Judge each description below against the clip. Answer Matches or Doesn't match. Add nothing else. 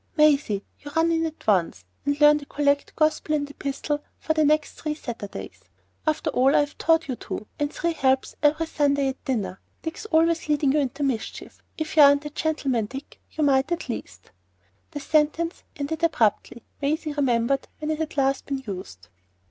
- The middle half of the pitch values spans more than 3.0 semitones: Doesn't match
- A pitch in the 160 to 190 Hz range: Doesn't match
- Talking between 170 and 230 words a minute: Matches